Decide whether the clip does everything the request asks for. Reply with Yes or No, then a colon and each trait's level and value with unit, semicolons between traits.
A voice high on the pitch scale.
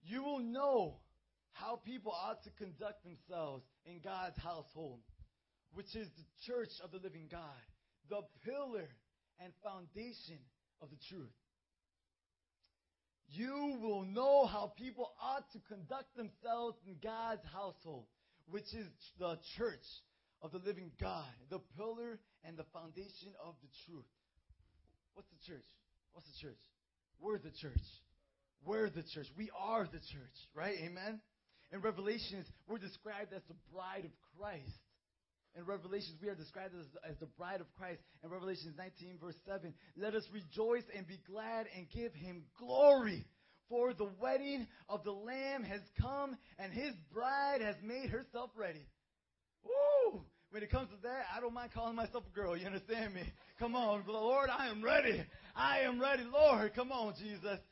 Yes: high, 195 Hz